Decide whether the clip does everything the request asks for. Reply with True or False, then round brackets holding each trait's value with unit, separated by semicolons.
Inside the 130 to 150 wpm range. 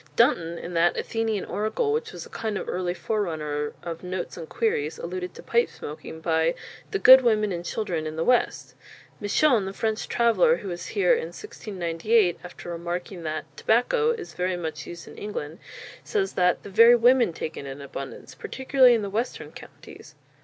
False (180 wpm)